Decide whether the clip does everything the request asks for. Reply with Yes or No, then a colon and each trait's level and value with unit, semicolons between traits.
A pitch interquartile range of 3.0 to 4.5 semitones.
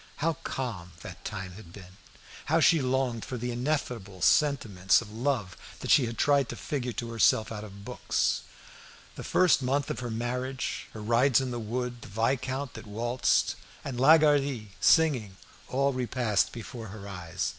Yes: average, 4.1 semitones